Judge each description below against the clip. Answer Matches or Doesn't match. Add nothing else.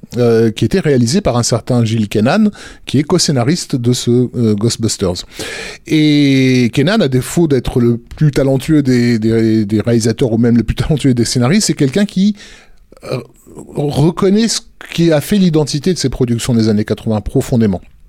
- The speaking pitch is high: Doesn't match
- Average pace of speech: Matches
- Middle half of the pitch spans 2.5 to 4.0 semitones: Doesn't match